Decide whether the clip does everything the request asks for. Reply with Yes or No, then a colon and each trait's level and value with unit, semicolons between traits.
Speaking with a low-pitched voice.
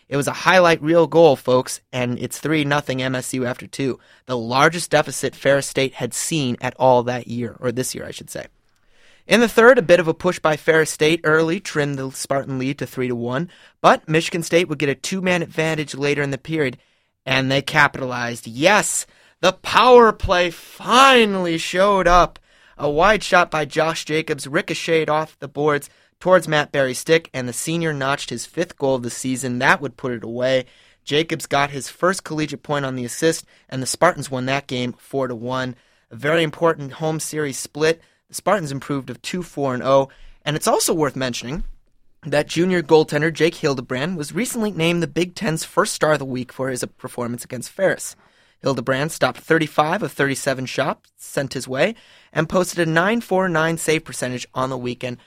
No: medium, 145 Hz